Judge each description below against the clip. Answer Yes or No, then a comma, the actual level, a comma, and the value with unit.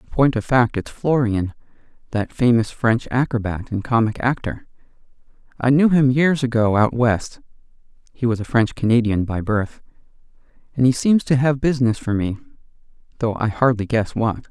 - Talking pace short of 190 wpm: Yes, average, 165 wpm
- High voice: No, low, 120 Hz